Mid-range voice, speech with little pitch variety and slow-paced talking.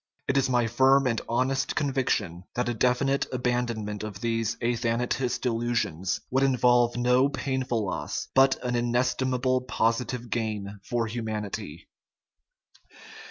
No: low, 120 Hz; narrow, 2.2 semitones; slow, 120 wpm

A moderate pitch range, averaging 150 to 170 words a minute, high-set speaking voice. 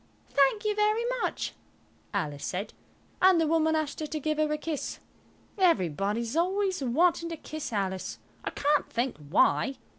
No: wide, 6.9 semitones; average, 160 wpm; very high, 300 Hz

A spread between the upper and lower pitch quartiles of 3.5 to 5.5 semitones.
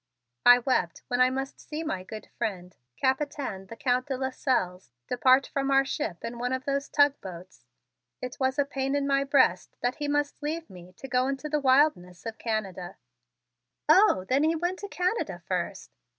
Yes: average, 4.7 semitones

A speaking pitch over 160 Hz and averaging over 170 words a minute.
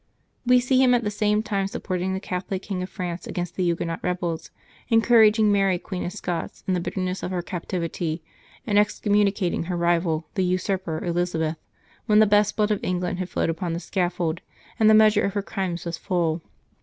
Yes: medium, 185 Hz; average, 195 wpm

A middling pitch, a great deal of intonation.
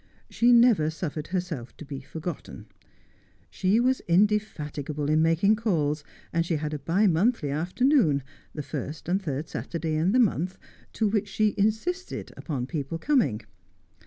Yes: medium, 170 Hz; wide, 5.9 semitones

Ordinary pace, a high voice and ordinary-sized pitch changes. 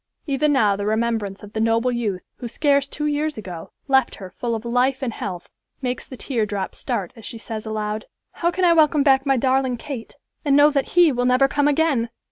No: fast, 220 wpm; very high, 250 Hz; average, 4.5 semitones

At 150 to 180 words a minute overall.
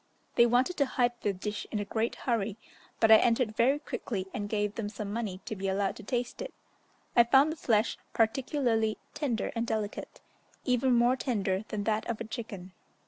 No: average, 195 wpm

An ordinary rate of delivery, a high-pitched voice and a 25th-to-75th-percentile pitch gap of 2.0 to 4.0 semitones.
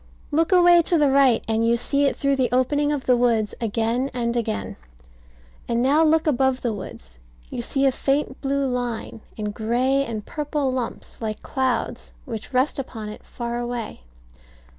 Yes: average, 175 wpm; very high, 250 Hz; average, 3.3 semitones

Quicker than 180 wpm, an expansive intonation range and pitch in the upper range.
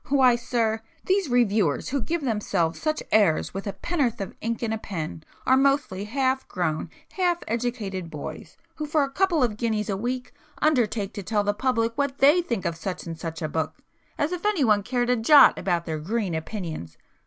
Yes: average, 195 wpm; wide, 5.9 semitones; high, 225 Hz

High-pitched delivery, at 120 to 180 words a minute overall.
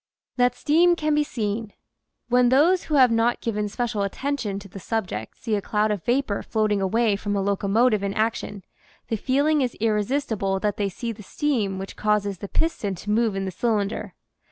No: high, 215 Hz; average, 190 wpm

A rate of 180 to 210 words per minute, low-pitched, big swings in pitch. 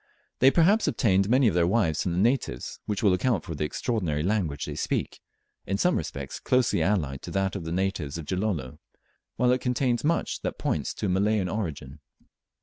Yes: average, 195 wpm; very low, 95 Hz; wide, 6.3 semitones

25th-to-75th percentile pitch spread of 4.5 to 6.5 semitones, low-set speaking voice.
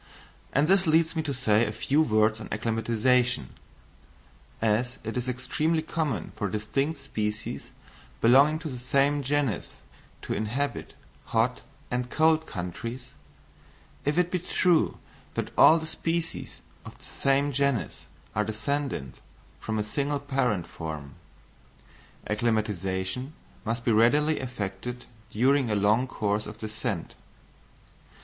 Yes: average, 5.0 semitones; low, 125 Hz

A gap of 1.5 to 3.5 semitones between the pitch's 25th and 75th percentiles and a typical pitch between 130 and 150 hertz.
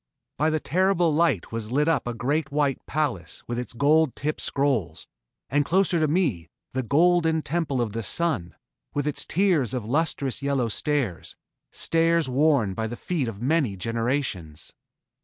No: average, 5.1 semitones; medium, 140 Hz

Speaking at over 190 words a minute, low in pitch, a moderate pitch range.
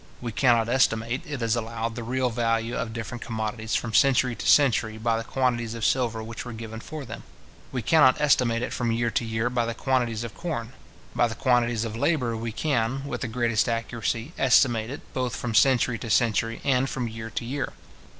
No: fast, 205 wpm; low, 120 Hz; narrow, 2.0 semitones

